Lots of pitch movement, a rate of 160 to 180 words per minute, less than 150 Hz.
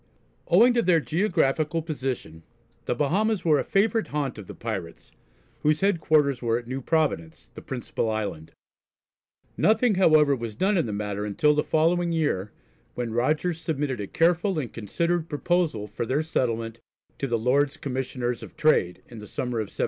Yes: wide, 6.3 semitones; average, 170 wpm; medium, 140 Hz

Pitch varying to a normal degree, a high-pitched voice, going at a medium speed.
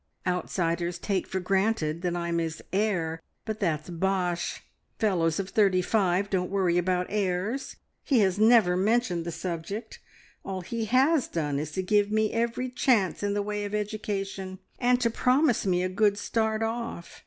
Yes: average, 3.6 semitones; high, 195 Hz; average, 165 wpm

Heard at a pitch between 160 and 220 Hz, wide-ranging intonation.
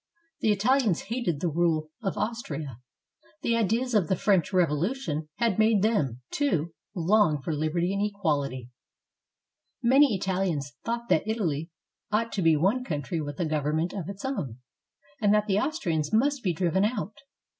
Yes: high, 190 Hz; wide, 5.9 semitones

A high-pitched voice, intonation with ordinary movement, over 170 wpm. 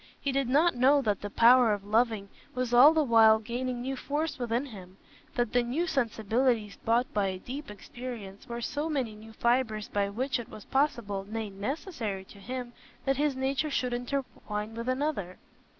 Yes: high, 240 Hz; average, 3.9 semitones; average, 180 wpm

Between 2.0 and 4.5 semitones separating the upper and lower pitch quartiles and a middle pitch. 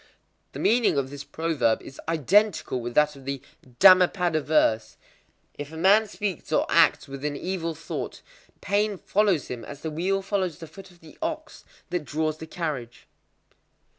No: average, 5.0 semitones; medium, 160 Hz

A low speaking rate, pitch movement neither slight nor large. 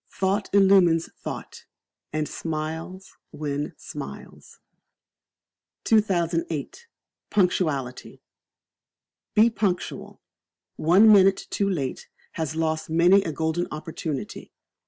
Yes: slow, 85 wpm; average, 3.8 semitones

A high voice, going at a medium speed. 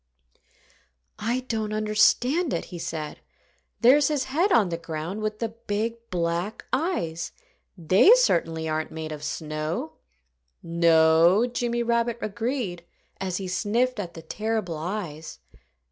No: high, 205 Hz; slow, 130 wpm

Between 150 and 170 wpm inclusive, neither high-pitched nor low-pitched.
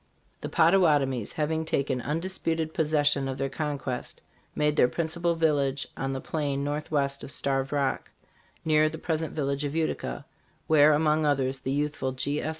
Yes: average, 160 wpm; medium, 150 Hz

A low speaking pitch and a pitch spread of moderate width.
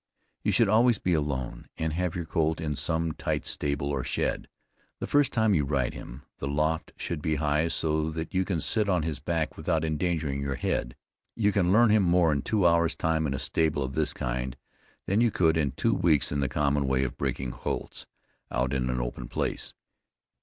Yes: very low, 80 Hz; average, 3.8 semitones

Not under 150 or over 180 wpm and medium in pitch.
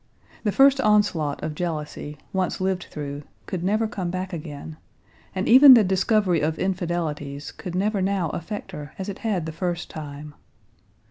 Yes: average, 160 wpm; medium, 180 Hz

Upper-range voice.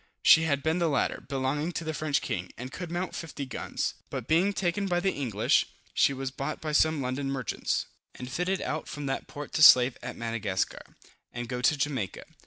No: medium, 145 Hz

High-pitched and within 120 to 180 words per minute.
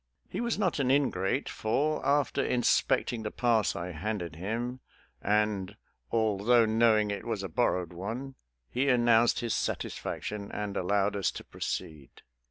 No: low, 110 Hz; average, 145 wpm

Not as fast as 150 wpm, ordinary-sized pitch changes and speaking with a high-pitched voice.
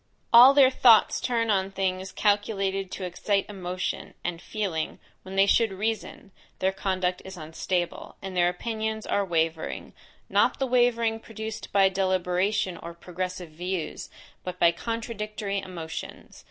Yes: average, 140 wpm; average, 3.2 semitones; high, 195 Hz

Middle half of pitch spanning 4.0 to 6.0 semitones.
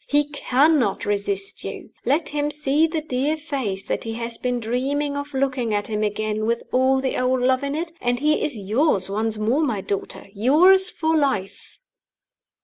Yes: average, 5.2 semitones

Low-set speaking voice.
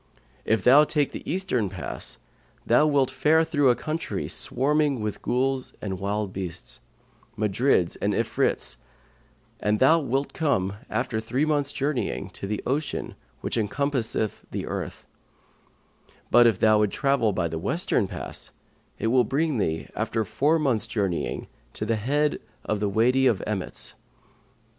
Yes: low, 120 Hz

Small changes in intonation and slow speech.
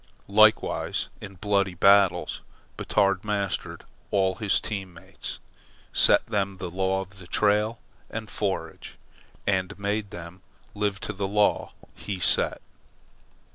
Yes: narrow, 1.7 semitones; slow, 120 wpm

